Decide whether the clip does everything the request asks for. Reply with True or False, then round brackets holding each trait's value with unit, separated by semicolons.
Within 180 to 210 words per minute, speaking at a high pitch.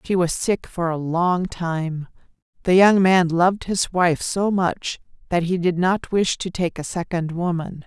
False (190 wpm; 175 Hz)